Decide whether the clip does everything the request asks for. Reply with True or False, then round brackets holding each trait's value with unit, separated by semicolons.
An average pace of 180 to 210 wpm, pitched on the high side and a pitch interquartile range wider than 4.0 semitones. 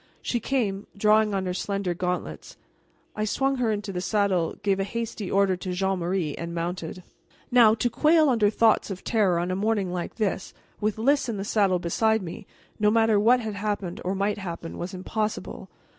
False (190 wpm; 200 Hz; 3.1 semitones)